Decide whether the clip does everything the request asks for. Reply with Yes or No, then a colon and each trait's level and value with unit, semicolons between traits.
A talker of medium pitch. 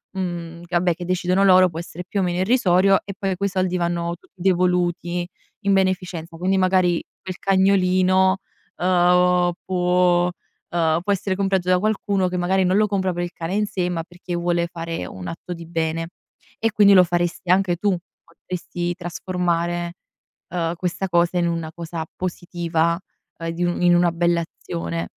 Yes: medium, 180 Hz